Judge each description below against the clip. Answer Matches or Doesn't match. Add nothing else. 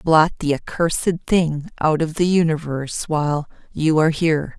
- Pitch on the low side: Doesn't match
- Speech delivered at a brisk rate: Doesn't match